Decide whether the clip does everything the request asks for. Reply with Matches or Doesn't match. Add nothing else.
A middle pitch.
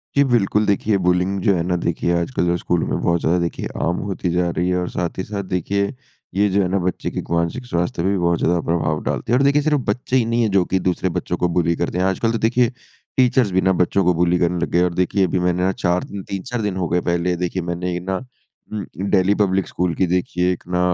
Doesn't match